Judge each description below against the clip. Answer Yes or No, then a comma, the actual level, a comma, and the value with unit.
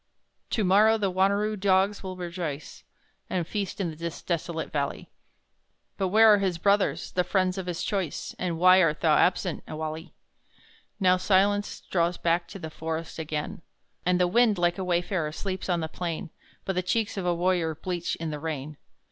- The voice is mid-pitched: Yes, medium, 180 Hz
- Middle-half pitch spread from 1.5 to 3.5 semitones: Yes, average, 2.8 semitones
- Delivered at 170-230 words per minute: Yes, average, 180 wpm